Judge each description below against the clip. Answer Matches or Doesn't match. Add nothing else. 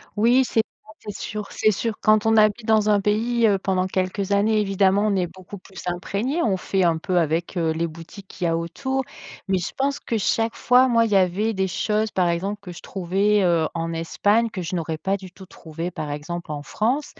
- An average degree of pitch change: Matches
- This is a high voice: Matches